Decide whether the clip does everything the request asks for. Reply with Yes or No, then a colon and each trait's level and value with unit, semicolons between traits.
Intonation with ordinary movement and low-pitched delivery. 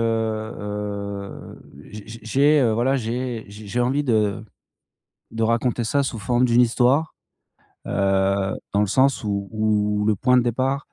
Yes: average, 3.2 semitones; low, 110 Hz